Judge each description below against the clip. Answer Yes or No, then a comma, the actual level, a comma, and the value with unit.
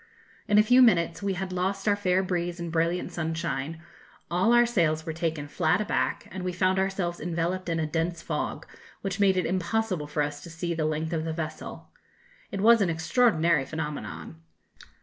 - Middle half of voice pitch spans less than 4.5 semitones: Yes, average, 3.1 semitones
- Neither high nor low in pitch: Yes, medium, 170 Hz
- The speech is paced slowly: No, average, 190 wpm